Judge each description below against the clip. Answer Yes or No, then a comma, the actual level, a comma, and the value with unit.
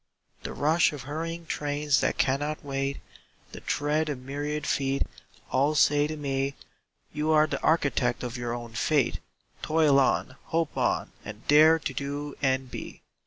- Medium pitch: Yes, medium, 145 Hz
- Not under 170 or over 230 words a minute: No, average, 160 wpm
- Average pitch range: No, narrow, 2.1 semitones